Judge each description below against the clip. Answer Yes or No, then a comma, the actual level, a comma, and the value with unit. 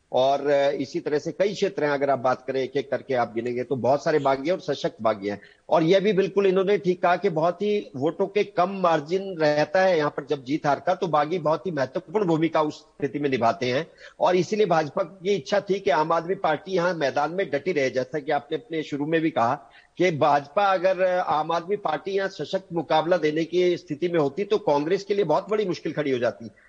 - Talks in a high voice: No, medium, 160 Hz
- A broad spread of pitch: No, average, 4.9 semitones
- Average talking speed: No, fast, 235 wpm